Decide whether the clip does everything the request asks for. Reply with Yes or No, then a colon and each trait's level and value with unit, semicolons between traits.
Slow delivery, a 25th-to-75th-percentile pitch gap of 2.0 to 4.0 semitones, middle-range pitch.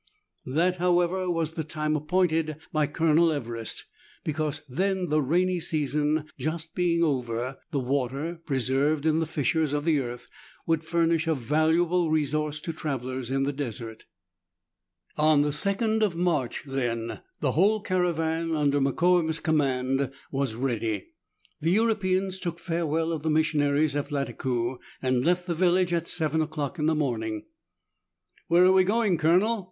No: average, 150 wpm; average, 3.6 semitones; medium, 155 Hz